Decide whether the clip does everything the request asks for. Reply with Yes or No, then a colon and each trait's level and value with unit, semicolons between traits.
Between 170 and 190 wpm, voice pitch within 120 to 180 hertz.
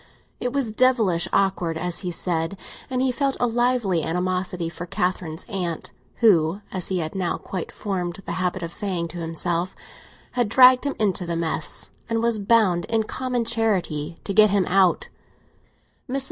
No: average, 175 wpm; high, 190 Hz